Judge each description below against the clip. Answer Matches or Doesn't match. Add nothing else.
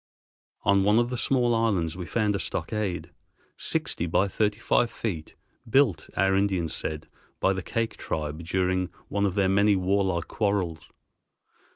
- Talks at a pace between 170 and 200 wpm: Doesn't match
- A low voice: Matches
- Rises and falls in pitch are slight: Doesn't match